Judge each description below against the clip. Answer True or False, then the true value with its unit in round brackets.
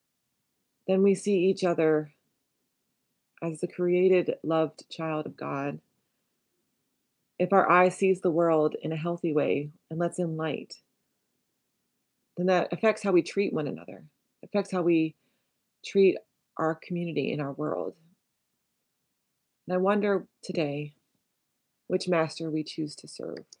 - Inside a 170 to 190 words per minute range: False (135 wpm)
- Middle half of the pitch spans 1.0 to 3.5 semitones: True (2.8 semitones)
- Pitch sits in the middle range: True (170 Hz)